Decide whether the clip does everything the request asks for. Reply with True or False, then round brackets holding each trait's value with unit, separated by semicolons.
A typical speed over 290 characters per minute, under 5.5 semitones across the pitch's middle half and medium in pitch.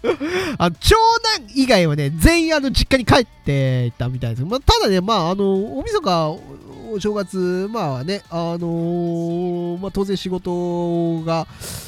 False (275 characters per minute; 5.1 semitones; 180 Hz)